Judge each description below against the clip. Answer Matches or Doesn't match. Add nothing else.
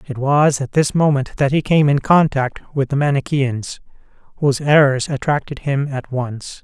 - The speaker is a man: Matches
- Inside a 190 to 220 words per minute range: Doesn't match